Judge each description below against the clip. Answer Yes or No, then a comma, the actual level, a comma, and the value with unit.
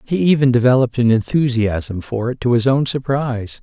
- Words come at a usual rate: Yes, average, 180 wpm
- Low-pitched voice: Yes, low, 125 Hz